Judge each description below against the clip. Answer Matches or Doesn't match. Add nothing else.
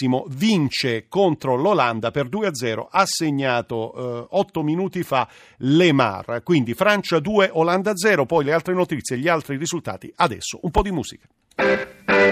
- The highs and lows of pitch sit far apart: Matches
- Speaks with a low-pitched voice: Doesn't match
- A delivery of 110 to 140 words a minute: Matches